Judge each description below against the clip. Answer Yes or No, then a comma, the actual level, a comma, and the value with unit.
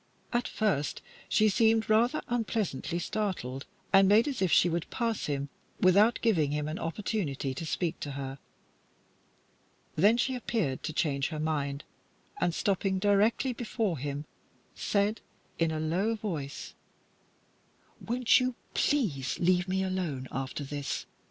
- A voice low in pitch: No, medium, 185 Hz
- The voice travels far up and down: Yes, wide, 6.8 semitones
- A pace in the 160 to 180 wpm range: No, average, 140 wpm